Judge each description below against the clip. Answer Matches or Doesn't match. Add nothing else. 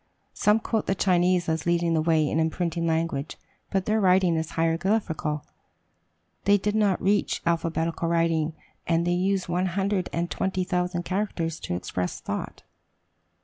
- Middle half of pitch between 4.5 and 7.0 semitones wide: Doesn't match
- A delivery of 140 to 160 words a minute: Matches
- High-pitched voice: Doesn't match